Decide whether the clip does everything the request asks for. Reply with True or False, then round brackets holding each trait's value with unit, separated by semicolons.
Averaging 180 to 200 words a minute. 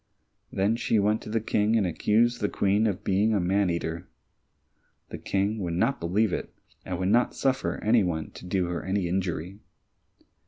True (185 wpm)